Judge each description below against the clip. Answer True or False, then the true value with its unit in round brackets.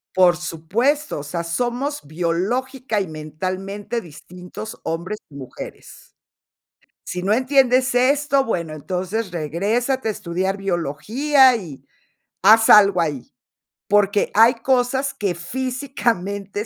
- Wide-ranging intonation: True (6.3 semitones)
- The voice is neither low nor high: False (200 Hz)